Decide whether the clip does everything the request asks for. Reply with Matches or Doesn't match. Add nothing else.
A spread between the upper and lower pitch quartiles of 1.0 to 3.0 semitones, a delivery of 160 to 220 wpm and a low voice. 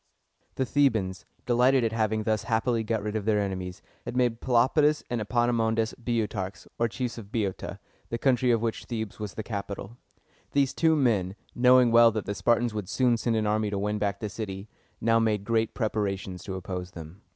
Matches